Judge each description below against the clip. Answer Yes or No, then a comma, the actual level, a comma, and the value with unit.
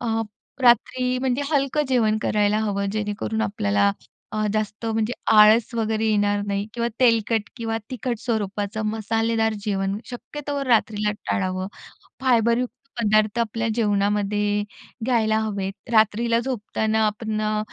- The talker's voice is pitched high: Yes, high, 220 Hz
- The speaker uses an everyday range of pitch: No, narrow, 2.0 semitones